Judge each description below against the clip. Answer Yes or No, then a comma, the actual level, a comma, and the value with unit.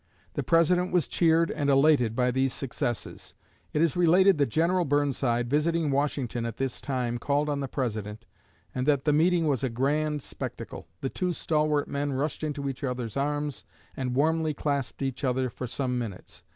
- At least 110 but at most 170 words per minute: No, average, 180 wpm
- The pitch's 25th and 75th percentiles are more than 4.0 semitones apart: No, average, 3.3 semitones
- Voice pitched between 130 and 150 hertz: Yes, medium, 140 Hz